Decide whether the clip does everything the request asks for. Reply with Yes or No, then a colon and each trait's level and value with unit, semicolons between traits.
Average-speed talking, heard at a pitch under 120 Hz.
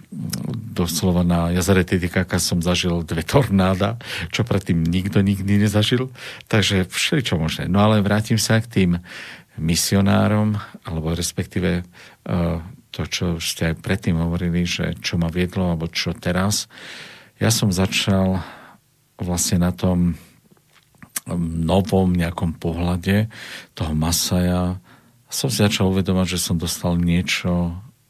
Yes: average, 120 wpm; very low, 90 Hz